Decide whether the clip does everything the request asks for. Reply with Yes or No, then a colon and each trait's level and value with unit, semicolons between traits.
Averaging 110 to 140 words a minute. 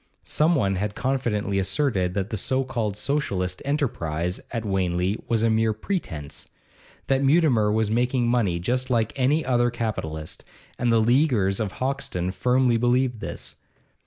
No: average, 150 wpm